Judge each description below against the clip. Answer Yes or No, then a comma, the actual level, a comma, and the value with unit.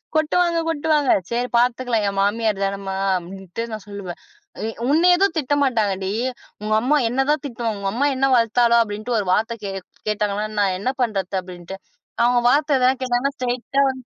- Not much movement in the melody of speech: No, average, 4.9 semitones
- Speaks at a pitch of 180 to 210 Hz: No, high, 235 Hz